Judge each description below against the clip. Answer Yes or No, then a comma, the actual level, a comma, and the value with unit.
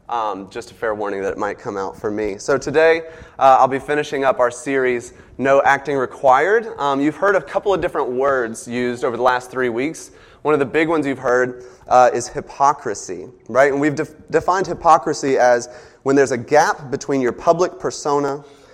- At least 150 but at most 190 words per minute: No, average, 200 wpm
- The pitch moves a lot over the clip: No, average, 4.0 semitones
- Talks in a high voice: No, medium, 140 Hz